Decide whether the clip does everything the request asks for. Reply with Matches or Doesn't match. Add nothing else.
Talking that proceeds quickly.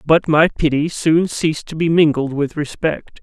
Doesn't match